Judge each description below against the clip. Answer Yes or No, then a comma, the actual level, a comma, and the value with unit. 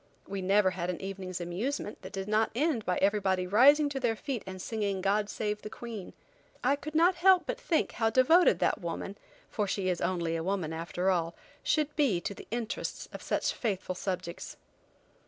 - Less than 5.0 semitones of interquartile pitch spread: No, average, 5.3 semitones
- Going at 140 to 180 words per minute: No, average, 190 wpm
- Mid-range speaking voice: No, high, 205 Hz